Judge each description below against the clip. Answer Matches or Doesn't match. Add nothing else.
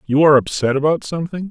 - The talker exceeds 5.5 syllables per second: Matches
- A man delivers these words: Matches